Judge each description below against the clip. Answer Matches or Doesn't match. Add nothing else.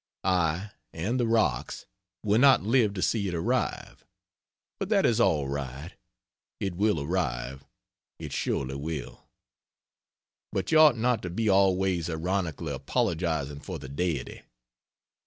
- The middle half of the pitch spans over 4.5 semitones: Matches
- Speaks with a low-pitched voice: Matches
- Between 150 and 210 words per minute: Doesn't match